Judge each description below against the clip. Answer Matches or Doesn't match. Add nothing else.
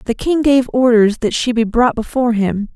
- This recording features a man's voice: Doesn't match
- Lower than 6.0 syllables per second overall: Matches